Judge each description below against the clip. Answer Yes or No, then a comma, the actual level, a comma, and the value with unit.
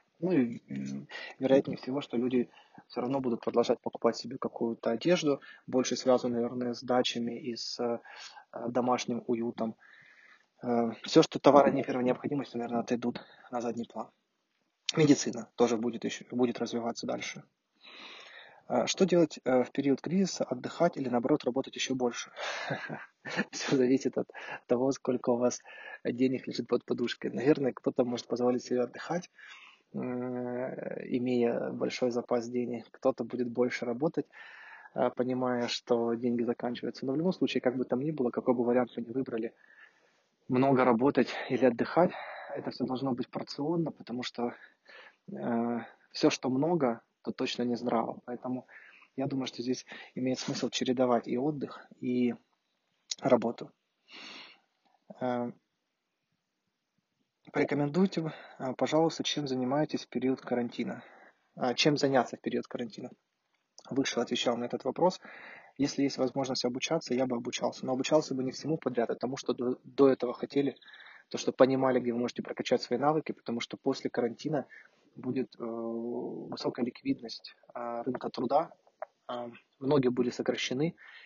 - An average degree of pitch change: No, narrow, 1.8 semitones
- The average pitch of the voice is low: Yes, low, 125 Hz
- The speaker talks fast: No, average, 140 wpm